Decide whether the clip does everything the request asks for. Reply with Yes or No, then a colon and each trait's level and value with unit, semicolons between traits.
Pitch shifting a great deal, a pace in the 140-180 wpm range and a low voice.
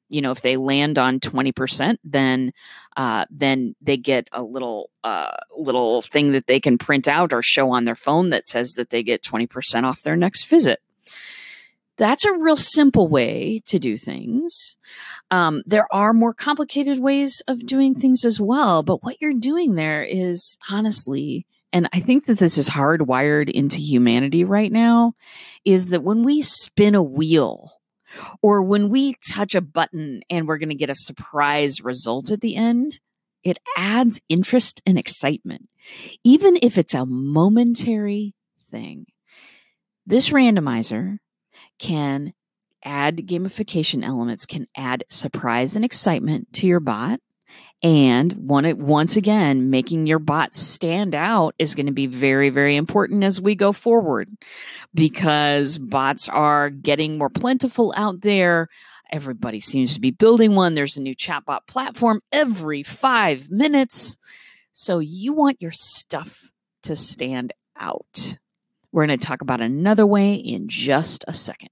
No: wide, 7.9 semitones; average, 155 wpm; medium, 175 Hz